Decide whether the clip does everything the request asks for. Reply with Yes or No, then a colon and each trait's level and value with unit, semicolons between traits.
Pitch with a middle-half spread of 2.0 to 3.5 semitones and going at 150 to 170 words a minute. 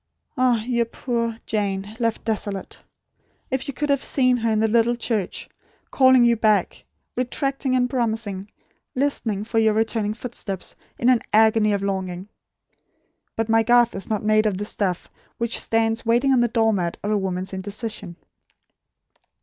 Yes: narrow, 2.6 semitones; average, 160 wpm